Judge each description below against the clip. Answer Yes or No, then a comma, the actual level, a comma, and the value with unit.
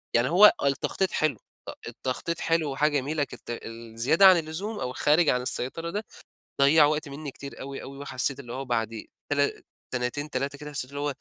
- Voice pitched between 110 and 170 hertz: Yes, medium, 140 Hz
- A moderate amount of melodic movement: Yes, average, 3.3 semitones